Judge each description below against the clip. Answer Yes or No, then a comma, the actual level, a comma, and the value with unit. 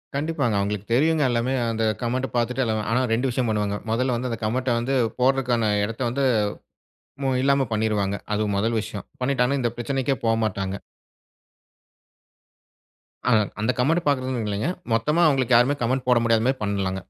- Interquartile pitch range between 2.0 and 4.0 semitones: Yes, average, 3.2 semitones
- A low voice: Yes, low, 120 Hz